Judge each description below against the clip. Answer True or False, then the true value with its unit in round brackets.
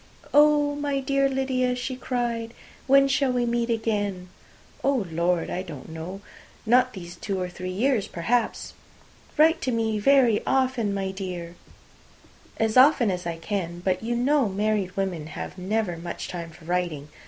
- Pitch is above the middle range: True (215 Hz)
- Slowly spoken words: False (160 wpm)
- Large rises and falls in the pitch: True (6.0 semitones)